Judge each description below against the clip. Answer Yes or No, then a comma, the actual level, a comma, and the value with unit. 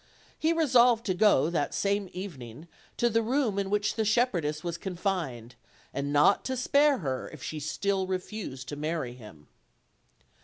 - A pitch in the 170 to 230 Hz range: Yes, medium, 185 Hz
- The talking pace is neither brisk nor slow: Yes, average, 160 wpm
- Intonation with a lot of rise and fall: Yes, wide, 6.9 semitones